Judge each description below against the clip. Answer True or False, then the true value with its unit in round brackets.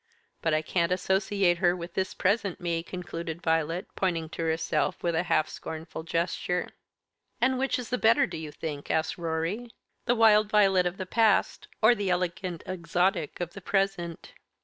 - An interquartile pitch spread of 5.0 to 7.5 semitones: False (3.1 semitones)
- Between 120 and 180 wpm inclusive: True (170 wpm)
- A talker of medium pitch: True (180 Hz)